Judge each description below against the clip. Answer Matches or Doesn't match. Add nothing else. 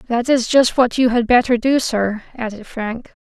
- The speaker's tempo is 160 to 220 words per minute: Matches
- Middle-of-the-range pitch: Doesn't match